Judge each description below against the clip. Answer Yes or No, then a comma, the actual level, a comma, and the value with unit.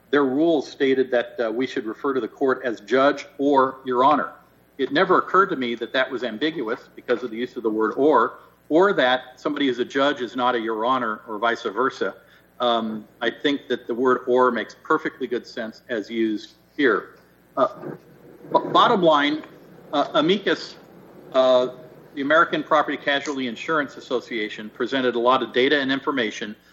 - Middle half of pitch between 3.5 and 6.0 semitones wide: No, average, 2.8 semitones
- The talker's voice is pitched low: Yes, low, 125 Hz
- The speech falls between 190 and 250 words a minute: No, average, 180 wpm